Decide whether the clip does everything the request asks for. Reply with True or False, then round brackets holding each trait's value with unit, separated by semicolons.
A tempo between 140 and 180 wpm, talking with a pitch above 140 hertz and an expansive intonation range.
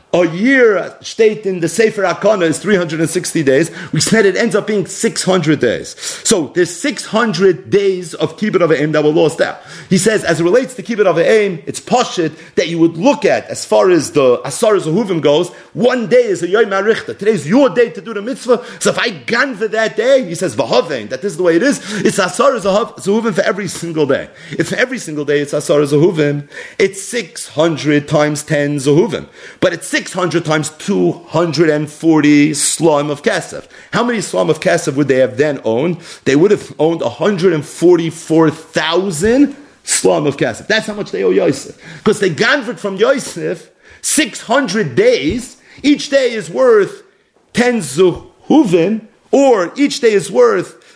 True (175 wpm; 190 Hz; 6.4 semitones)